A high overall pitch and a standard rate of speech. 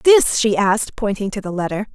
No: high, 215 Hz; fast, 215 wpm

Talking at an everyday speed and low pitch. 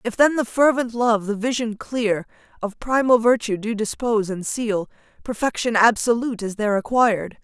No: average, 160 wpm; high, 225 Hz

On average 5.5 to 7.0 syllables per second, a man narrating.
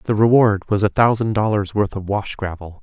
No: 5.0 syllables/s; male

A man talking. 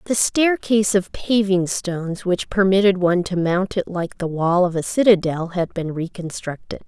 No: female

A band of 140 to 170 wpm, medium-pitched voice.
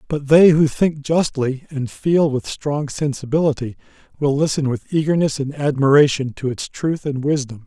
Yes: average, 165 wpm; medium, 145 Hz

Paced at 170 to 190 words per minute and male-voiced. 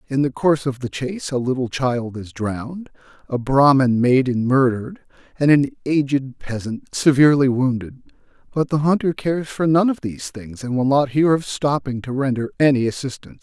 Yes: average, 180 wpm; male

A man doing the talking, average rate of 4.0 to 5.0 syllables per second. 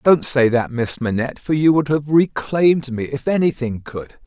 Yes: male; 4.8 syllables/s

